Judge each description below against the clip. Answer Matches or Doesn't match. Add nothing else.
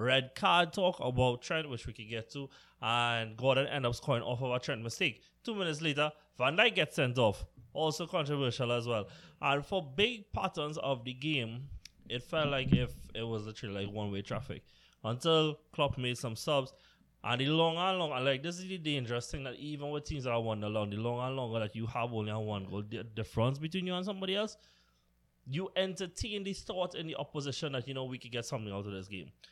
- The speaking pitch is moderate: Doesn't match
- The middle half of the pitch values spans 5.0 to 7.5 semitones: Matches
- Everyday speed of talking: Doesn't match